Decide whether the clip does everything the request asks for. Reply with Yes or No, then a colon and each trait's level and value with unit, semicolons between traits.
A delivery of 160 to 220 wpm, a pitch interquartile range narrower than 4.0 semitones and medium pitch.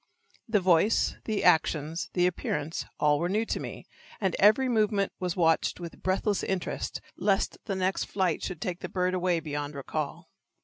Yes: average, 170 wpm; average, 3.3 semitones; medium, 180 Hz